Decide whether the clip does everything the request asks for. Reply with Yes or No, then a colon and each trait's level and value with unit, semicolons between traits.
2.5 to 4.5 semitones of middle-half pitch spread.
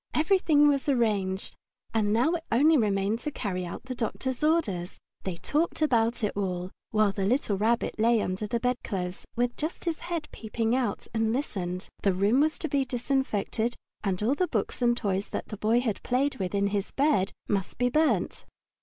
No: wide, 5.4 semitones